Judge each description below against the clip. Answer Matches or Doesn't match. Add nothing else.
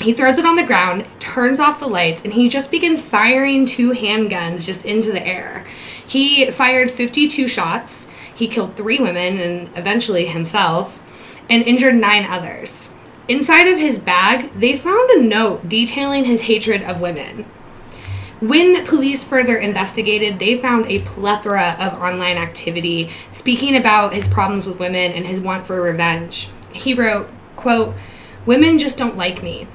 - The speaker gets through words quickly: Doesn't match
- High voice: Matches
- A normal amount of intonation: Doesn't match